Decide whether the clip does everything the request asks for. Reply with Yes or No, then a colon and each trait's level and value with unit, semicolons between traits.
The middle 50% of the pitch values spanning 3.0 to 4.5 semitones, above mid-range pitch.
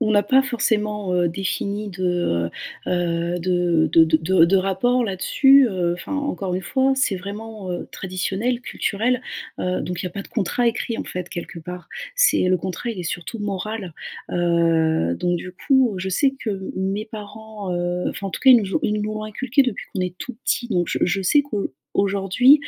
Yes: average, 3.9 semitones; high, 195 Hz